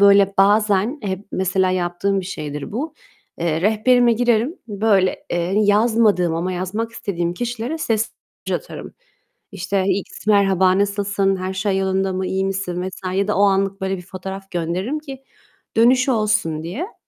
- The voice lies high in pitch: Yes, high, 195 Hz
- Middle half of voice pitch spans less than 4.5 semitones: Yes, average, 2.7 semitones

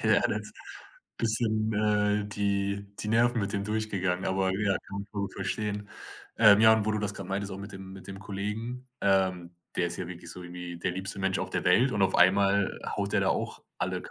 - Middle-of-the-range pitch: No, low, 100 Hz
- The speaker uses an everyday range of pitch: No, narrow, 1.9 semitones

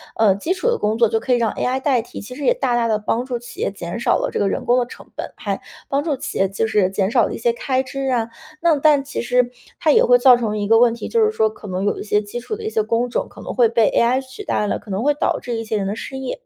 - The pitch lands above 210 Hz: Yes, high, 240 Hz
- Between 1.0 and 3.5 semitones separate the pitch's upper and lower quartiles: No, average, 3.9 semitones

